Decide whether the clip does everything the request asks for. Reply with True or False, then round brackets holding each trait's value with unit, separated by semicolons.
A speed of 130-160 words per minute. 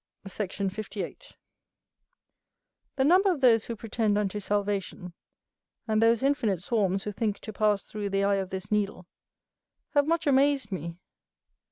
True (145 wpm)